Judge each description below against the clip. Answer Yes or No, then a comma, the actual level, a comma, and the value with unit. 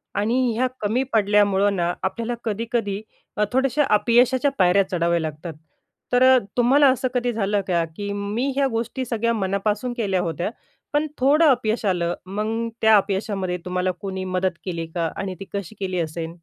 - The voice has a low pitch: No, high, 205 Hz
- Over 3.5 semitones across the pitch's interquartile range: Yes, average, 4.2 semitones